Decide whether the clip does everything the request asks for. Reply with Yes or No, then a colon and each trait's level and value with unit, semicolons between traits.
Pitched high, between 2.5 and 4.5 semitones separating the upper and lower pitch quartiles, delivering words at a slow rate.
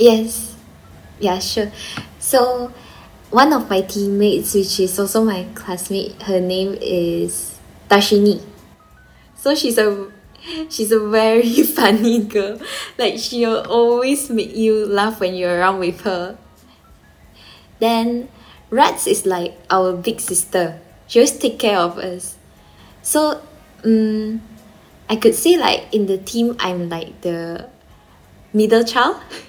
Yes: high, 210 Hz; average, 4.2 semitones; slow, 130 wpm